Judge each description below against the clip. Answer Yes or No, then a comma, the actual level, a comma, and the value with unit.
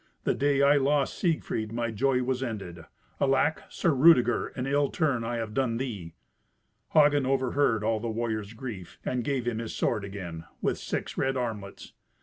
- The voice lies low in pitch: Yes, low, 120 Hz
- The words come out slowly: No, average, 170 wpm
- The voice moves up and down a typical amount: Yes, average, 3.8 semitones